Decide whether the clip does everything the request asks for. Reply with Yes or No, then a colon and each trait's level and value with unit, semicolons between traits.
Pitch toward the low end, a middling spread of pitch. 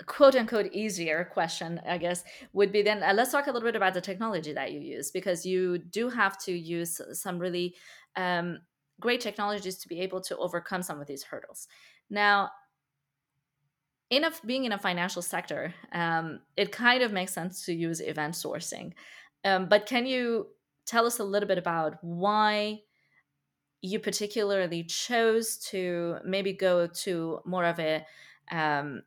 No: medium, 185 Hz; average, 3.7 semitones